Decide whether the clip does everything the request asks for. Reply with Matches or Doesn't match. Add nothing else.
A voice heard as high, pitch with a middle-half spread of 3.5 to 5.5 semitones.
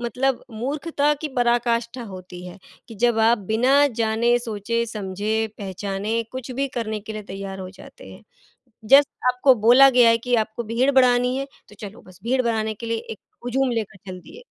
Doesn't match